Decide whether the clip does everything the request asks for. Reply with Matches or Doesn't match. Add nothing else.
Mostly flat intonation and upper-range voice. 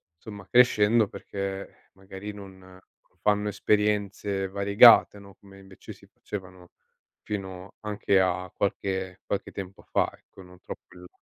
Doesn't match